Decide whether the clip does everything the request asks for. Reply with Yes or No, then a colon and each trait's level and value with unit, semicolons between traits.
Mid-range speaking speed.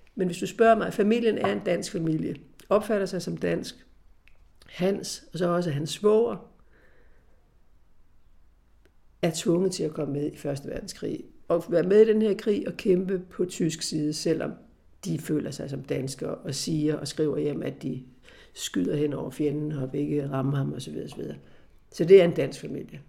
Yes: average, 180 wpm